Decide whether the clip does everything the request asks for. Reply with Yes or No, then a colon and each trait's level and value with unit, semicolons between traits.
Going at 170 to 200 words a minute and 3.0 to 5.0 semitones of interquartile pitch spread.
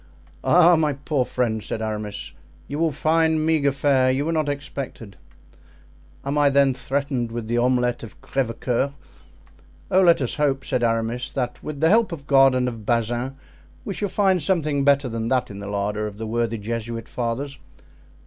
Yes: average, 175 wpm; average, 4.0 semitones